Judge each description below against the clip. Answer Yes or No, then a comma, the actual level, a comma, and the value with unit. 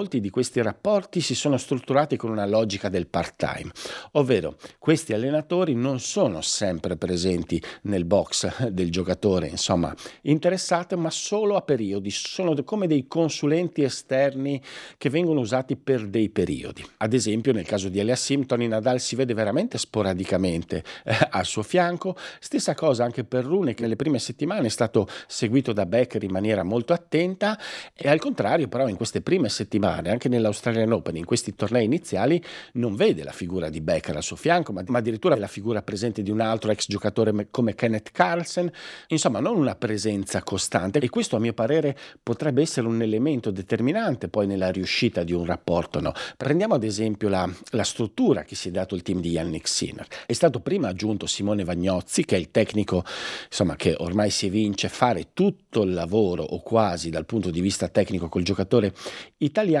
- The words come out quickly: Yes, fast, 180 wpm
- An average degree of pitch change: No, wide, 5.9 semitones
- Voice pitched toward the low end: Yes, low, 115 Hz